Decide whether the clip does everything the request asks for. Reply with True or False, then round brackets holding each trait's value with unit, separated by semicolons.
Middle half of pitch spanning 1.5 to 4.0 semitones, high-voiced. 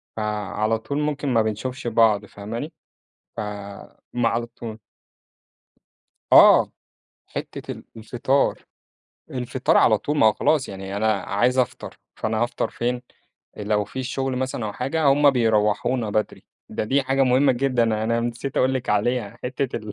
False (3.4 semitones; 120 Hz)